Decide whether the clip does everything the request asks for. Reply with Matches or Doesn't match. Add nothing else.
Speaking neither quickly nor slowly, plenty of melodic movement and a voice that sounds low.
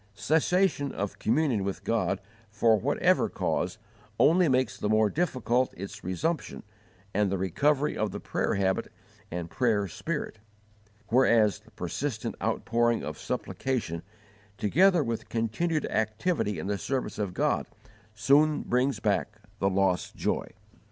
Doesn't match